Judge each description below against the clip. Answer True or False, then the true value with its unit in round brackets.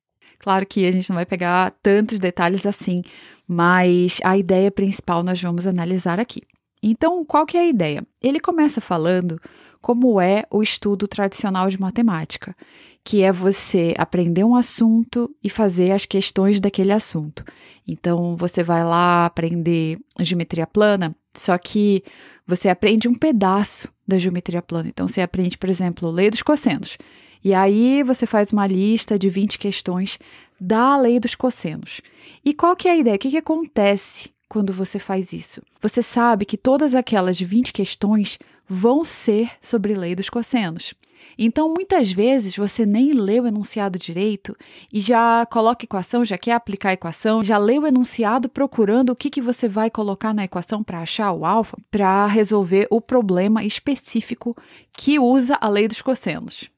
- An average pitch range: True (4.2 semitones)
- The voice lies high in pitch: True (205 Hz)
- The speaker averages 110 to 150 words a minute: False (165 wpm)